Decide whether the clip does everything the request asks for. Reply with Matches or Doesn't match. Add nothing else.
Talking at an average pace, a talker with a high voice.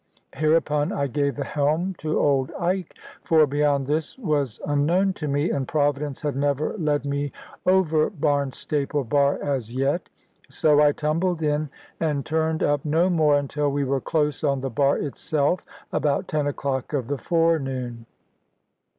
Doesn't match